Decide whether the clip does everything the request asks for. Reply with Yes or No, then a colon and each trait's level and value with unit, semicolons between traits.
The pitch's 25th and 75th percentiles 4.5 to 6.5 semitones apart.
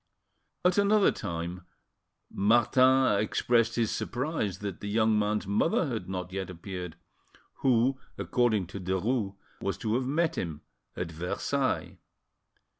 Yes: average, 5.1 semitones